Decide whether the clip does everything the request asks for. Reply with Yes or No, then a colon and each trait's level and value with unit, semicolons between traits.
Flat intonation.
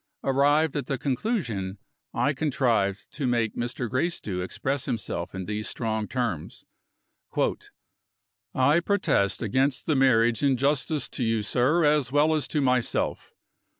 No: average, 4.4 semitones